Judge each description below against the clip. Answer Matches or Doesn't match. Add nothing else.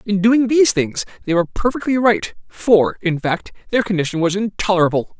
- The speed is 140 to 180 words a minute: Matches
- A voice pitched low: Doesn't match